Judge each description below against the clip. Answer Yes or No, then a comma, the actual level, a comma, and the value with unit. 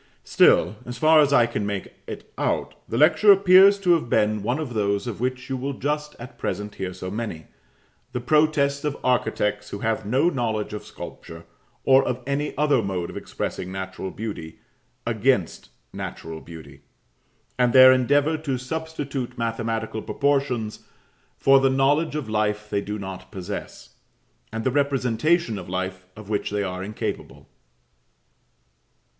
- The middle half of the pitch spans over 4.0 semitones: Yes, average, 5.3 semitones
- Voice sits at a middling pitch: No, low, 120 Hz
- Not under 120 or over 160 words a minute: Yes, average, 155 wpm